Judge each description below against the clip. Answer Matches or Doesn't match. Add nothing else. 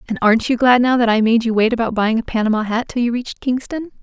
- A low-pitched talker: Doesn't match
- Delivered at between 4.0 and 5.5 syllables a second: Doesn't match